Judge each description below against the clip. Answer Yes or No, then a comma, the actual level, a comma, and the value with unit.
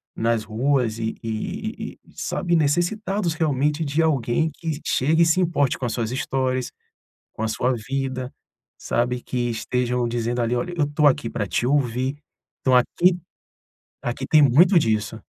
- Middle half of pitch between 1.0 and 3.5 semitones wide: No, average, 4.5 semitones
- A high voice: No, low, 130 Hz